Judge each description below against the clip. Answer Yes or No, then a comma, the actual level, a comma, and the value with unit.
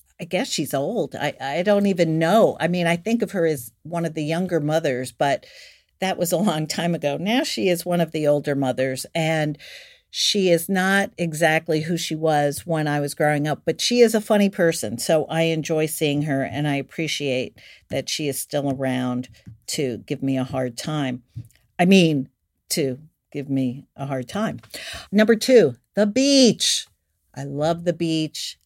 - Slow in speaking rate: No, average, 190 wpm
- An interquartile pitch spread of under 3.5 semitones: No, average, 4.3 semitones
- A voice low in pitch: No, medium, 155 Hz